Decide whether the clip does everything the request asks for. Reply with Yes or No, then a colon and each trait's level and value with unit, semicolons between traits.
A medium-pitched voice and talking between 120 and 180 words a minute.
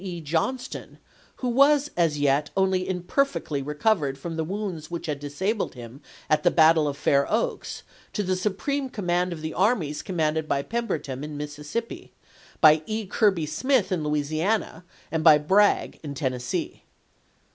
Yes: medium, 165 Hz; average, 160 wpm